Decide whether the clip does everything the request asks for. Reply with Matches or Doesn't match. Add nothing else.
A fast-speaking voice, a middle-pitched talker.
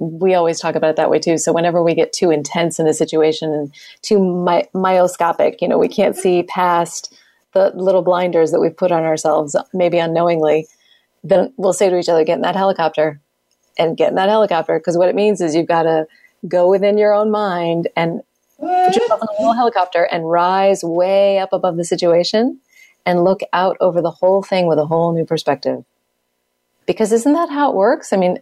Matches